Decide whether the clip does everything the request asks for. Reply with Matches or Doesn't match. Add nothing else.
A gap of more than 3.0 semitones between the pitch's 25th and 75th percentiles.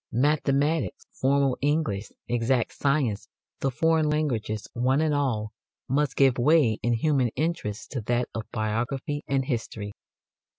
Matches